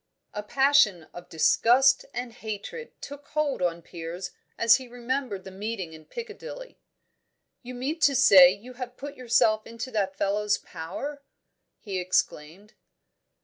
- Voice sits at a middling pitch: No, high, 230 Hz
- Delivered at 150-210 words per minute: No, average, 140 wpm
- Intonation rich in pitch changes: Yes, wide, 6.1 semitones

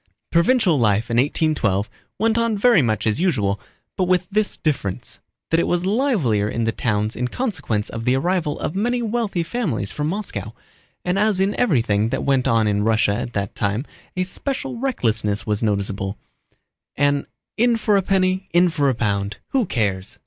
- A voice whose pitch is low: No, medium, 145 Hz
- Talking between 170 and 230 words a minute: Yes, average, 175 wpm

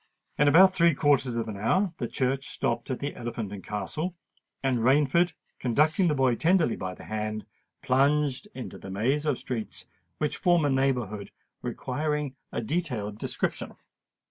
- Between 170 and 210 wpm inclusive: No, average, 160 wpm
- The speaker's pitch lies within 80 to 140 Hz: Yes, low, 135 Hz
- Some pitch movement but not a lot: Yes, average, 4.9 semitones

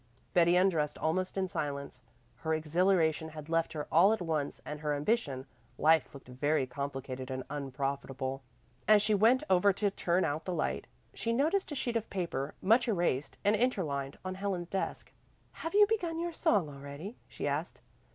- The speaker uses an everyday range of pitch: No, wide, 6.1 semitones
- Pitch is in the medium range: Yes, medium, 165 Hz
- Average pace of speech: Yes, average, 170 wpm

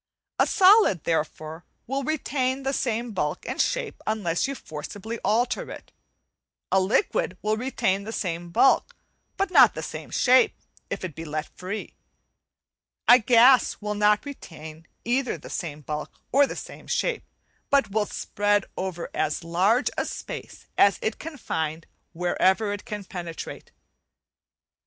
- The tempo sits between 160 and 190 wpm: No, average, 145 wpm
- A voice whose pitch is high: Yes, high, 210 Hz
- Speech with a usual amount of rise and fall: No, wide, 7.0 semitones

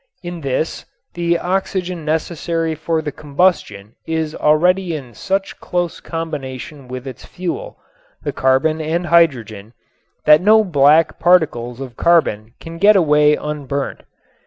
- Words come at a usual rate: No, slow, 130 wpm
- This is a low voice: No, medium, 155 Hz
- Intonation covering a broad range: No, average, 4.0 semitones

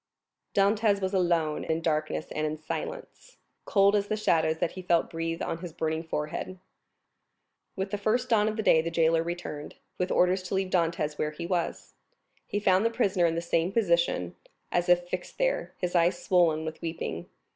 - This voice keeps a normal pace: Yes, average, 180 wpm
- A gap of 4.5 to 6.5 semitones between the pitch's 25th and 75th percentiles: No, average, 3.2 semitones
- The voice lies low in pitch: No, medium, 175 Hz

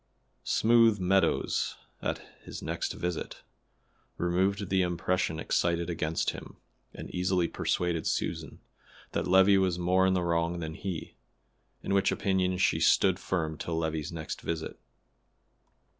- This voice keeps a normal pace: No, slow, 130 wpm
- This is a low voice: Yes, very low, 90 Hz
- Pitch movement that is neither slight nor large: No, narrow, 2.2 semitones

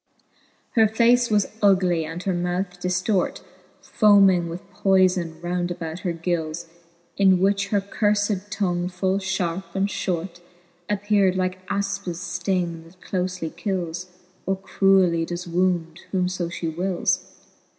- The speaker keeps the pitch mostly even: Yes, narrow, 2.1 semitones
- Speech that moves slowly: Yes, slow, 130 wpm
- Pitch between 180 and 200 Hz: Yes, medium, 185 Hz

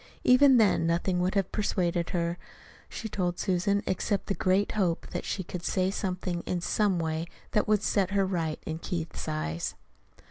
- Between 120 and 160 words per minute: No, average, 175 wpm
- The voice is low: No, medium, 185 Hz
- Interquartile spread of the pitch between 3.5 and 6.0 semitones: No, average, 2.8 semitones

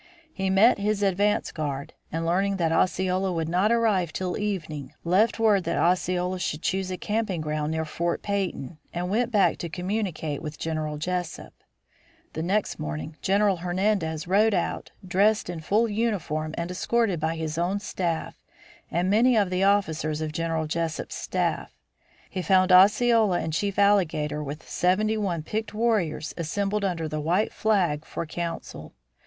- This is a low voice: No, medium, 180 Hz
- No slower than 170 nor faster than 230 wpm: No, average, 160 wpm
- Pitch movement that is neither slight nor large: Yes, average, 4.1 semitones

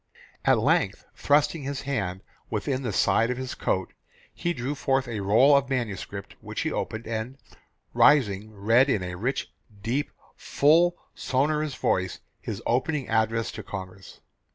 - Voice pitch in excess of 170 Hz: No, low, 120 Hz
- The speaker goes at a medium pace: Yes, average, 150 wpm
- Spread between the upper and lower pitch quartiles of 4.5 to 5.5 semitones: Yes, average, 5.1 semitones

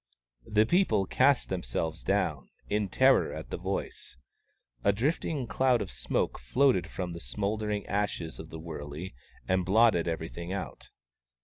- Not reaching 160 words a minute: Yes, average, 140 wpm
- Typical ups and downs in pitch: Yes, average, 4.7 semitones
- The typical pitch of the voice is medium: No, low, 100 Hz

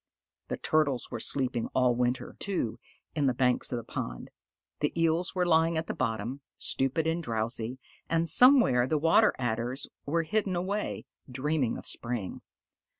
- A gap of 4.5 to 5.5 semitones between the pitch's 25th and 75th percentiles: Yes, average, 5.2 semitones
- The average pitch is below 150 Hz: Yes, low, 135 Hz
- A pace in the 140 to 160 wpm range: Yes, average, 155 wpm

